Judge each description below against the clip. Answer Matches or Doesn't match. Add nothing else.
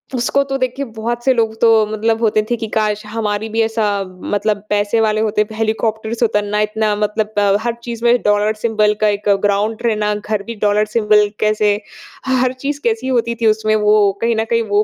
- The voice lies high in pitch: Matches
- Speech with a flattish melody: Matches